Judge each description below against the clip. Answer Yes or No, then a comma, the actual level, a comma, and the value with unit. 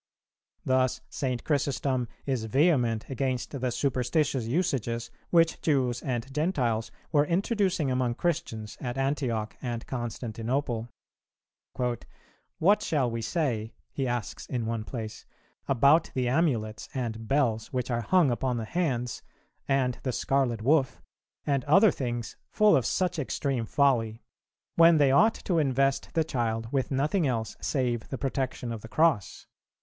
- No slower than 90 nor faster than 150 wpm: Yes, average, 140 wpm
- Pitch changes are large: No, average, 3.6 semitones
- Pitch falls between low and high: No, low, 130 Hz